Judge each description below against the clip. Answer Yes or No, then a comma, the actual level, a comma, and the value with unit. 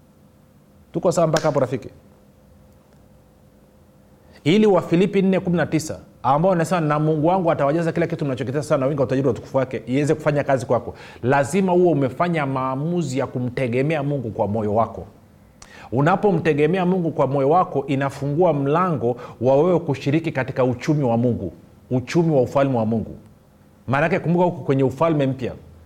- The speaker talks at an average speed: Yes, average, 130 wpm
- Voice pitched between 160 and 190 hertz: No, medium, 140 Hz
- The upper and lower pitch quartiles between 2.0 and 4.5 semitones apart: No, average, 5.0 semitones